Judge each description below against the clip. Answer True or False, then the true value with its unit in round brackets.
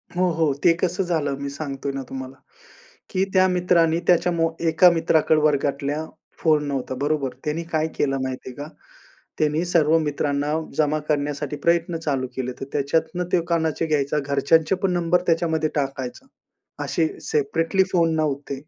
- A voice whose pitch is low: False (155 Hz)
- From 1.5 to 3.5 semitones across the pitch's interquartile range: True (2.9 semitones)